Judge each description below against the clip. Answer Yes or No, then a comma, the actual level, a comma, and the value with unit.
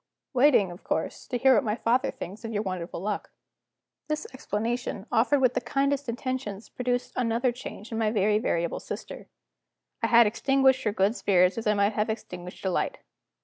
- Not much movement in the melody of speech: No, average, 3.8 semitones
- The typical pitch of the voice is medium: No, high, 230 Hz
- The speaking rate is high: No, average, 190 wpm